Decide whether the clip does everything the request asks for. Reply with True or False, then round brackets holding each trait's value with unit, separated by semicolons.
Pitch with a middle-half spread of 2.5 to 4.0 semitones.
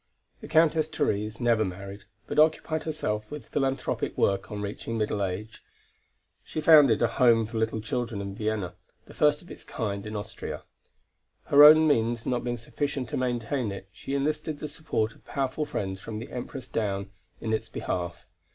False (5.5 semitones)